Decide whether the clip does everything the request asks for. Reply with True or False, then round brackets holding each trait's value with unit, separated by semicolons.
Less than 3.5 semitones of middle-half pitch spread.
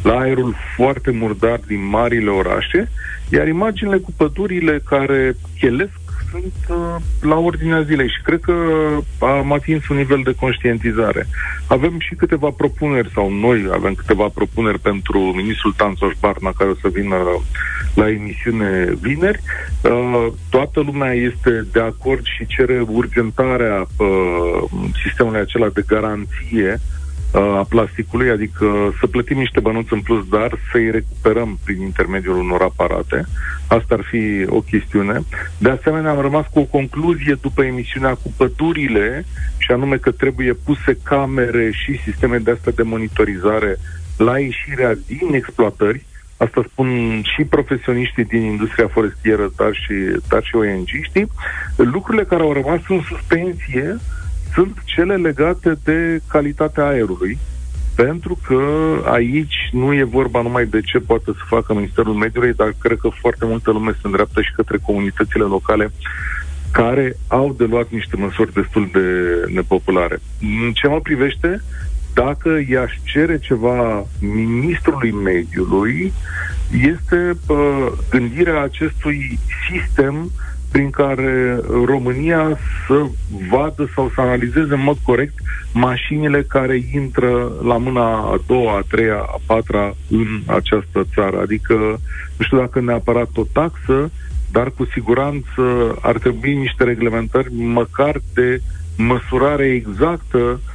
False (5.1 semitones)